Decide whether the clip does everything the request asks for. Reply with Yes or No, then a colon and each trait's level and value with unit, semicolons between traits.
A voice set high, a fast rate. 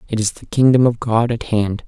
No: low, 115 Hz; fast, 255 wpm